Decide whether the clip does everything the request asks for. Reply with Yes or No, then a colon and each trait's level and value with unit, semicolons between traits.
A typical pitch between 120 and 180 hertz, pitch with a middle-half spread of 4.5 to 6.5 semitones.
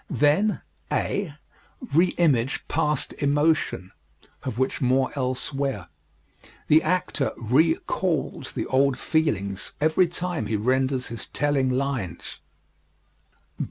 No: medium, 140 Hz; average, 3.7 semitones